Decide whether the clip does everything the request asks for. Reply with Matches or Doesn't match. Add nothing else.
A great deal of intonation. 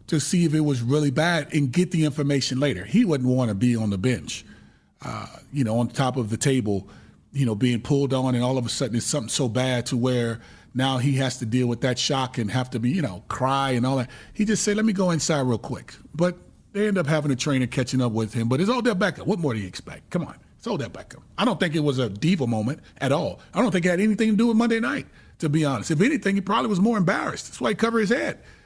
Matches